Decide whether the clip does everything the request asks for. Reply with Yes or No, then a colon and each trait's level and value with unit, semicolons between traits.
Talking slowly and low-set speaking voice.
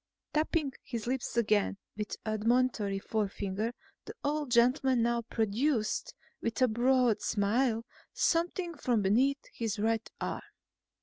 No: slow, 120 wpm; high, 235 Hz